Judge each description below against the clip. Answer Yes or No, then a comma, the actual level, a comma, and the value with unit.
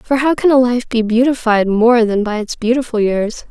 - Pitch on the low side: No, high, 235 Hz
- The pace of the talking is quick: Yes, fast, 225 wpm